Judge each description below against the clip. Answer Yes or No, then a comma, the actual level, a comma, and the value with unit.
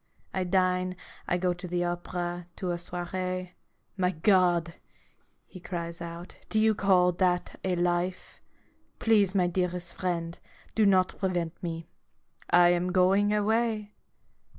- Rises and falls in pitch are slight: Yes, narrow, 1.3 semitones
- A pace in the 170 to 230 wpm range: No, slow, 135 wpm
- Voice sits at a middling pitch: Yes, medium, 180 Hz